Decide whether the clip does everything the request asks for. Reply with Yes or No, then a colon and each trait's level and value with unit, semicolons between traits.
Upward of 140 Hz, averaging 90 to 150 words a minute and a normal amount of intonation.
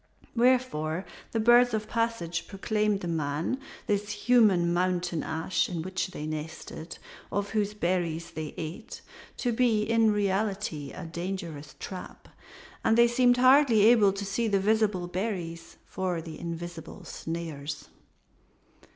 Yes: high, 190 Hz; slow, 135 wpm; average, 4.7 semitones